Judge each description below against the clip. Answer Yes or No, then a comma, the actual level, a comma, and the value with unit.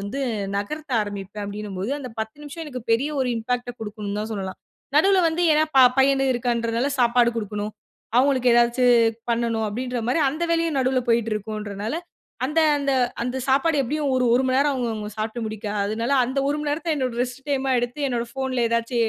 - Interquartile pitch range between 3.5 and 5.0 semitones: Yes, average, 3.8 semitones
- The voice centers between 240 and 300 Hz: Yes, high, 245 Hz